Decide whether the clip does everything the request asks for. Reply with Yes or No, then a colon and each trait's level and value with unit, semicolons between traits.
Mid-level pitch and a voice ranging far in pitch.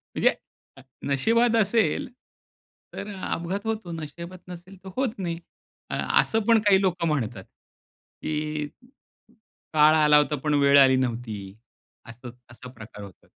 Yes: medium, 155 Hz; wide, 6.5 semitones